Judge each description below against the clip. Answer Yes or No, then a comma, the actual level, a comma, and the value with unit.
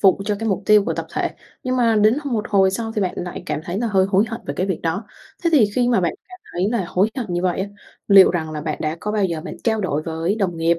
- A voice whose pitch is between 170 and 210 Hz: Yes, high, 195 Hz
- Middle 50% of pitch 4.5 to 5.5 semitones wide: No, average, 4.0 semitones